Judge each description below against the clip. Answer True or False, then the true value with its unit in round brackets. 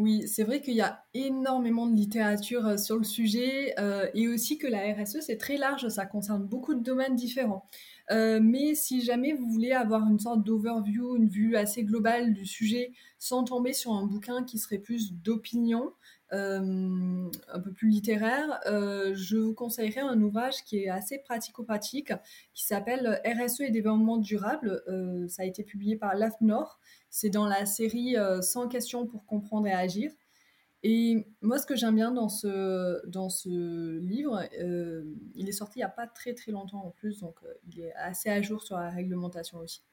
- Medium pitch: False (220 Hz)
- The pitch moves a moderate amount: True (3.3 semitones)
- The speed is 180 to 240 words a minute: True (190 wpm)